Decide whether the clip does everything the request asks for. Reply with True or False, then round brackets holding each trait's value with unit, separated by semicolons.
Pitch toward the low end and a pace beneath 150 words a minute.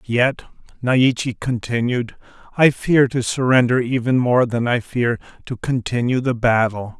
True (120 Hz; 135 wpm)